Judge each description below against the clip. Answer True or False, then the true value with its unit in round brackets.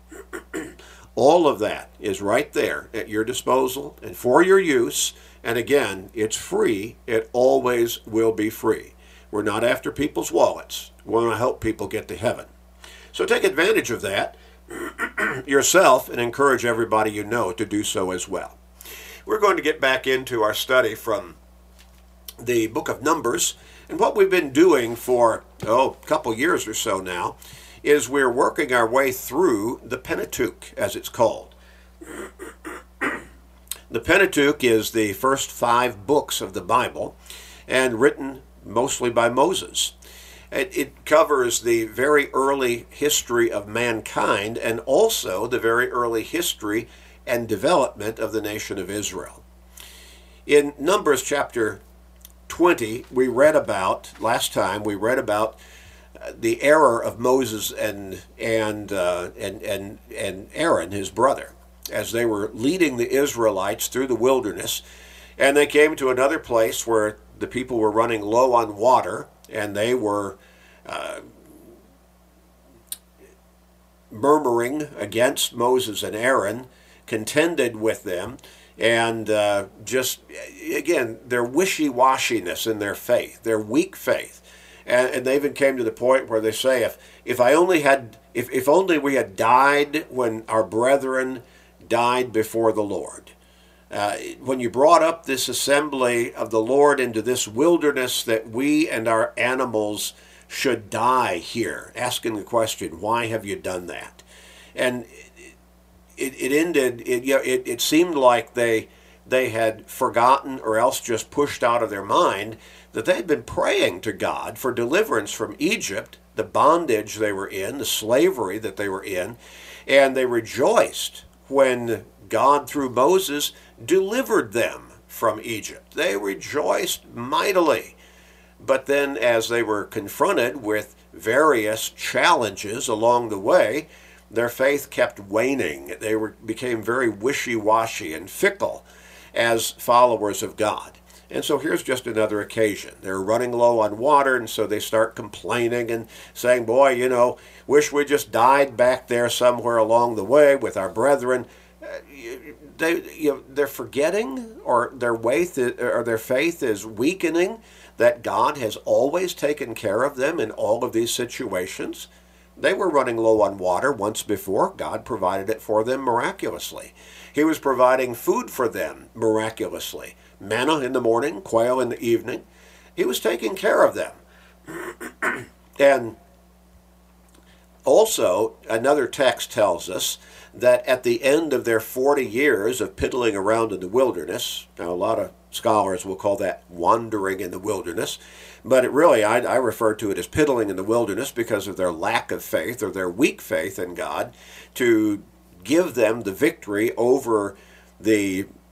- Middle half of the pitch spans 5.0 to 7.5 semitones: True (5.3 semitones)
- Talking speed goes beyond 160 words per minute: False (150 wpm)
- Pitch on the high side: False (120 Hz)